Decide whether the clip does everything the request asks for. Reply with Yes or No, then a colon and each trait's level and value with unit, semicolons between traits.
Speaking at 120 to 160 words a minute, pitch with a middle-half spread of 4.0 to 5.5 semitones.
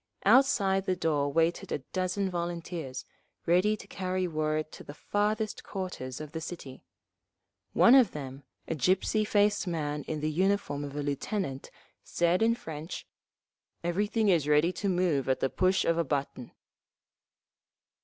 Yes: average, 150 wpm; average, 4.6 semitones